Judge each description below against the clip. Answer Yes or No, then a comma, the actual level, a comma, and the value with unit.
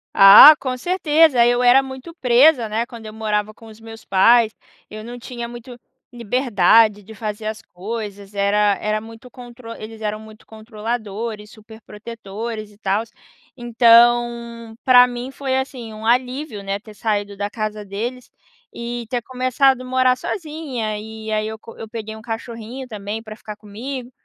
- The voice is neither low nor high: No, high, 225 Hz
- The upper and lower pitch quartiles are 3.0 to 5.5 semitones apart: No, narrow, 2.4 semitones